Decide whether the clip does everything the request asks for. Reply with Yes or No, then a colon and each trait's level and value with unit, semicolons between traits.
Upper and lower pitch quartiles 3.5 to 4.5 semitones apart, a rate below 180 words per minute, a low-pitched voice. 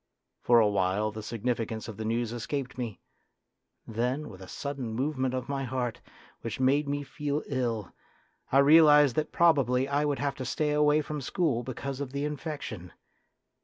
Yes: average, 3.9 semitones; average, 170 wpm; low, 130 Hz